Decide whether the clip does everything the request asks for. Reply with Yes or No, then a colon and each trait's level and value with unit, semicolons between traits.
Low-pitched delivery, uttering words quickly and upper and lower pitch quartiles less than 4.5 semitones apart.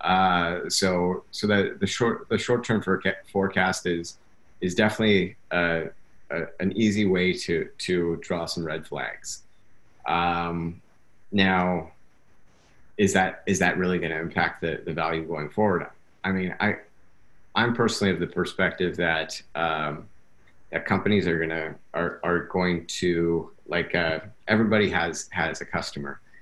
No: very low, 90 Hz; average, 145 wpm; narrow, 2.5 semitones